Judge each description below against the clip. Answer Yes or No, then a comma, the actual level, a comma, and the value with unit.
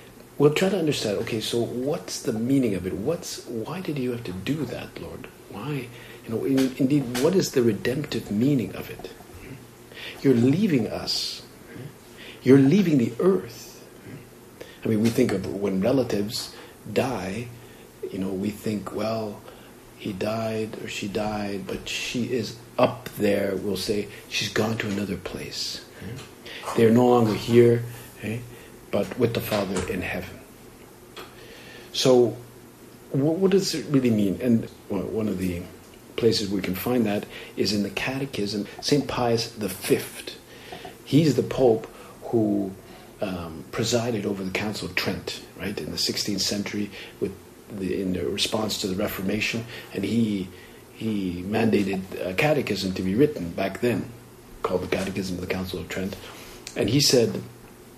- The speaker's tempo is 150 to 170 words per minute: Yes, average, 155 wpm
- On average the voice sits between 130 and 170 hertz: No, low, 115 Hz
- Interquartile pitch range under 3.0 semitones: No, average, 3.4 semitones